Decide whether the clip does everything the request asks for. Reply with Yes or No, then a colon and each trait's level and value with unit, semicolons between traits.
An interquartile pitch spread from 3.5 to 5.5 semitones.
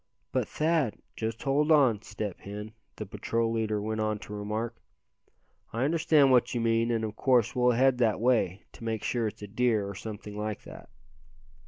No: average, 2.7 semitones